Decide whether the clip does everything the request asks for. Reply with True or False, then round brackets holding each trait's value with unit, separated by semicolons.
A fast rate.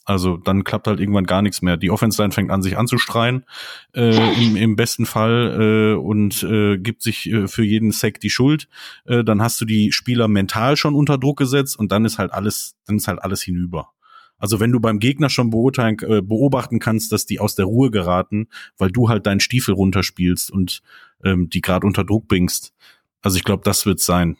True (210 wpm)